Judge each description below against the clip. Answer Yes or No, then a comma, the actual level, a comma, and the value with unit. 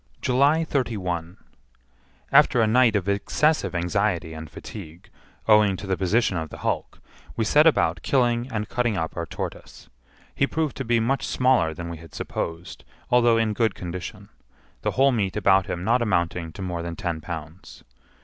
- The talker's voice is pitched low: Yes, low, 100 Hz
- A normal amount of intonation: No, wide, 5.9 semitones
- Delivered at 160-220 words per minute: Yes, average, 170 wpm